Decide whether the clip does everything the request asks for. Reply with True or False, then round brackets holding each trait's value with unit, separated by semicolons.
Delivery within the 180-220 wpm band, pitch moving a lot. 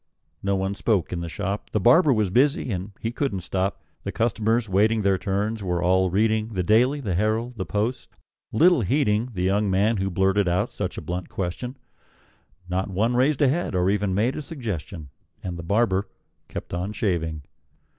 False (185 wpm; 3.5 semitones)